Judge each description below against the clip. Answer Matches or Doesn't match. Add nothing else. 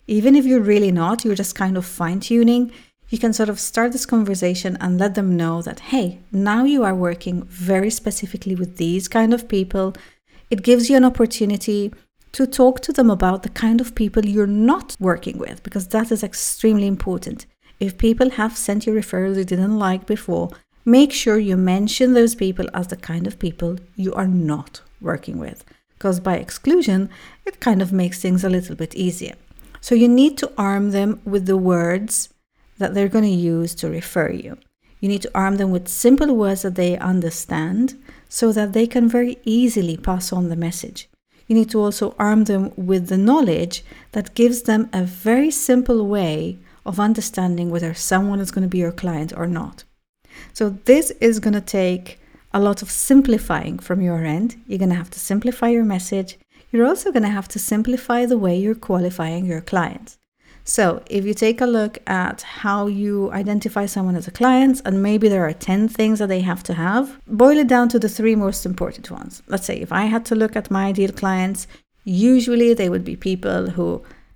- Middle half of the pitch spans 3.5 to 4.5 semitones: Matches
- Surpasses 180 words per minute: Matches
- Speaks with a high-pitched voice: Matches